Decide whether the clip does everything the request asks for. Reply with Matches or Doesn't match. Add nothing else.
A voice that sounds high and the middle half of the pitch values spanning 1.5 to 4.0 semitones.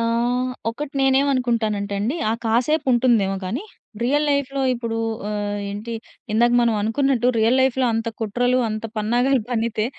Matches